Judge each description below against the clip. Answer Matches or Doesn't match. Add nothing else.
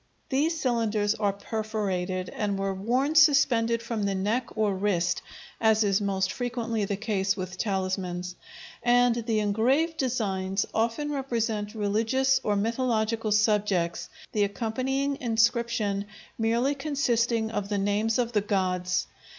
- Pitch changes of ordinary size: Matches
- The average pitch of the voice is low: Doesn't match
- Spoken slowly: Matches